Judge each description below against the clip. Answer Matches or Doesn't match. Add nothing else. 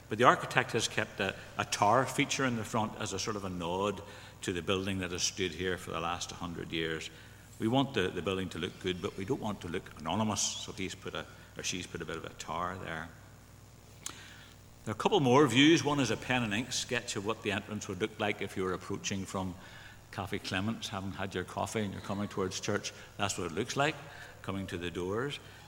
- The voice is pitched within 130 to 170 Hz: Doesn't match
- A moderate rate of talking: Doesn't match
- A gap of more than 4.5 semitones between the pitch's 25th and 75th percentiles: Doesn't match